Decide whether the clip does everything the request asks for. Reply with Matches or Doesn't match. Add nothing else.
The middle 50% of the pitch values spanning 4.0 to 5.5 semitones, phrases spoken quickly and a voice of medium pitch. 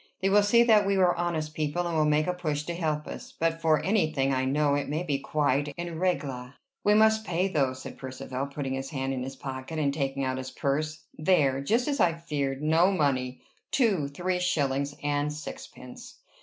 Matches